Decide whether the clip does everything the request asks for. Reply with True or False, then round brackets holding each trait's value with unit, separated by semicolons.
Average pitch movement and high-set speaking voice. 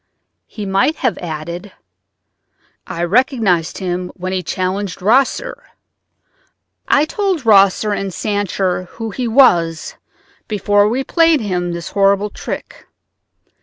True (4.4 semitones; 200 Hz)